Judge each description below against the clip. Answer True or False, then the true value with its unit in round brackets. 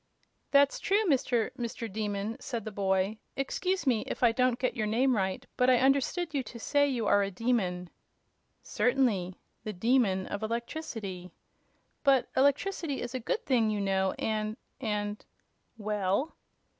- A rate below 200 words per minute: True (155 wpm)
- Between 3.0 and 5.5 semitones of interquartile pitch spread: True (4.5 semitones)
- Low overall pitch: False (230 Hz)